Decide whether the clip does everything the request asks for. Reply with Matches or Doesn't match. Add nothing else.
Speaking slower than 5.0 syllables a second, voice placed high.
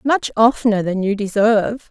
Doesn't match